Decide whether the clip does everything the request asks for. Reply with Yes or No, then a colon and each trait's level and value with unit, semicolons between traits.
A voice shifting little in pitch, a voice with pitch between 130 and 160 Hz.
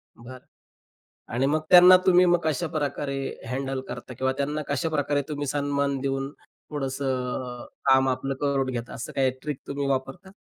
Yes: narrow, 2.0 semitones; medium, 140 Hz